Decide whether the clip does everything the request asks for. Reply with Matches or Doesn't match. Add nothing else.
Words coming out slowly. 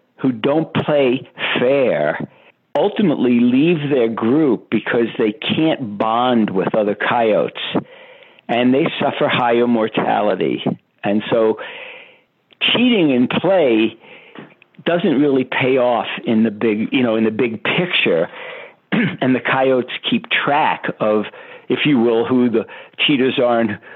Matches